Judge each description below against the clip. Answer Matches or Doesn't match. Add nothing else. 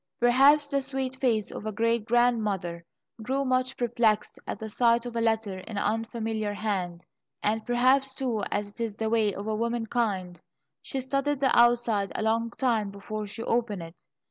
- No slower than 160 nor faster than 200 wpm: Matches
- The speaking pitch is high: Matches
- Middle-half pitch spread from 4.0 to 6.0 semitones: Doesn't match